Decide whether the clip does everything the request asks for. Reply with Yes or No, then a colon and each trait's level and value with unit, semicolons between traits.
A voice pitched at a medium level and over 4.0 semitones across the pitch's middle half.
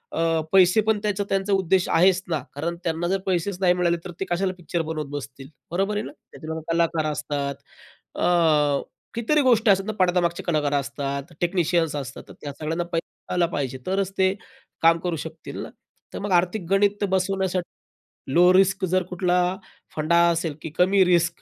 No: medium, 175 Hz; average, 2.9 semitones